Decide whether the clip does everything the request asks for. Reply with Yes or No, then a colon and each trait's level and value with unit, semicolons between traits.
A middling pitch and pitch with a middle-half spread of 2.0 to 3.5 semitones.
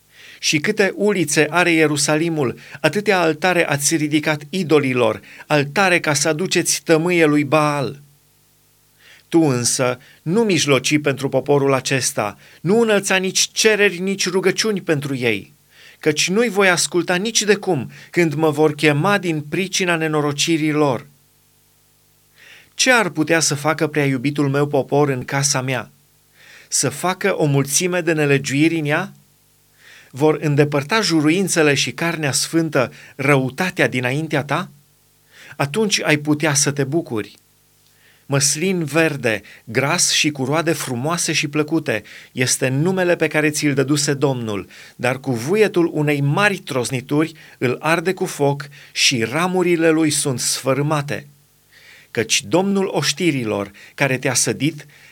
Yes: medium, 150 Hz; average, 3.2 semitones